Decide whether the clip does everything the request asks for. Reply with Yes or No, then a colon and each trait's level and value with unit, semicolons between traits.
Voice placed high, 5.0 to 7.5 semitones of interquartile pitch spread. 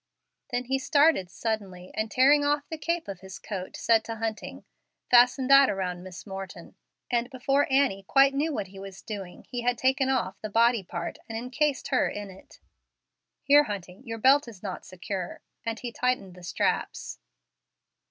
Yes: high, 230 Hz; wide, 5.6 semitones